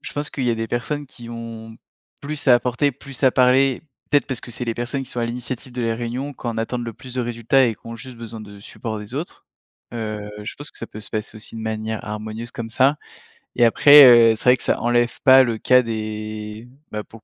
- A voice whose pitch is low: Yes, low, 120 Hz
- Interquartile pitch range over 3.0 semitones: No, narrow, 2.5 semitones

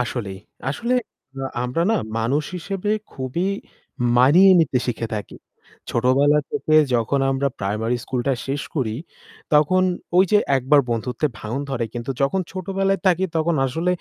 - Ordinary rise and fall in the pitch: No, wide, 6.2 semitones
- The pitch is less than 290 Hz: Yes, medium, 140 Hz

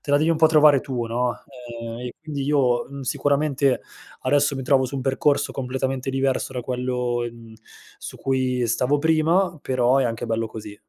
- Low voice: Yes, low, 130 Hz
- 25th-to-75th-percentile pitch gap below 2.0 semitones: No, narrow, 2.6 semitones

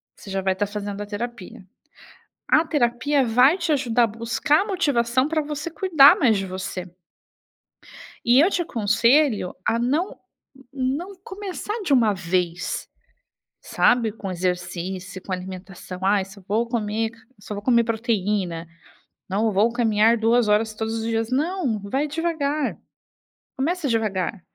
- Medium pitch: No, high, 230 Hz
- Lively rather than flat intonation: Yes, wide, 5.9 semitones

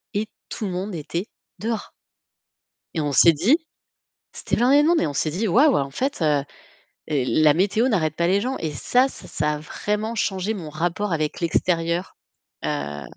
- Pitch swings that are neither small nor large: No, wide, 5.9 semitones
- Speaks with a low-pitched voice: No, medium, 180 Hz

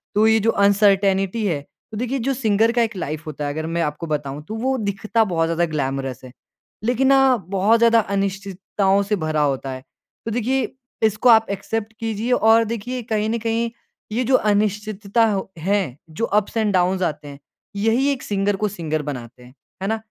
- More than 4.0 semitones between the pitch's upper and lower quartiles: Yes, average, 5.1 semitones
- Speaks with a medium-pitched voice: No, high, 205 Hz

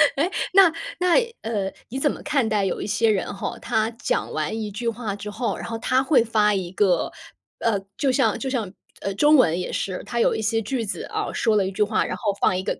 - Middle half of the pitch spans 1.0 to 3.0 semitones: No, average, 4.1 semitones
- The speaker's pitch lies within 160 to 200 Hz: No, high, 220 Hz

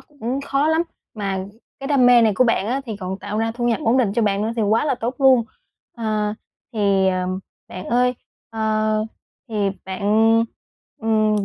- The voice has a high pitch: Yes, high, 220 Hz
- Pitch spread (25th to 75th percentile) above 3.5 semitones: No, average, 3.1 semitones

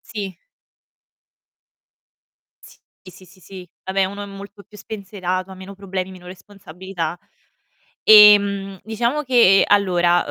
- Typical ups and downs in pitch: No, narrow, 1.7 semitones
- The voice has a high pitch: Yes, high, 195 Hz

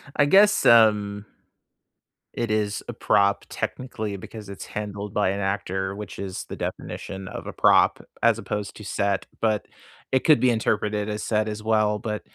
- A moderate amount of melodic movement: No, narrow, 1.5 semitones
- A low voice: Yes, low, 105 Hz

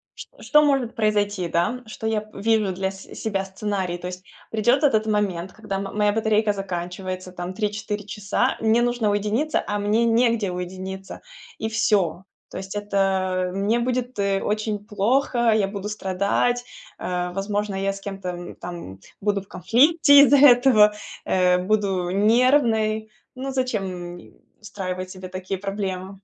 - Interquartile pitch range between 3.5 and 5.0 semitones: No, average, 2.9 semitones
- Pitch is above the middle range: Yes, high, 205 Hz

